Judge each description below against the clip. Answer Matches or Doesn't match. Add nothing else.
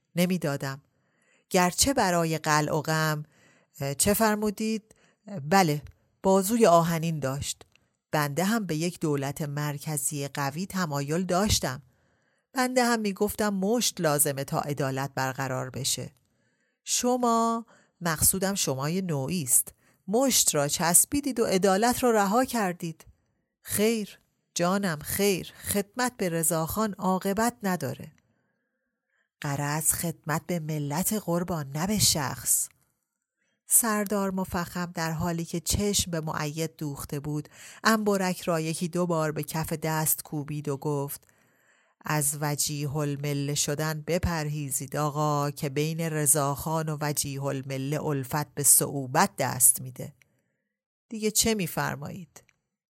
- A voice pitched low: Doesn't match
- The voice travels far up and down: Doesn't match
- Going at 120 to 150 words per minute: Doesn't match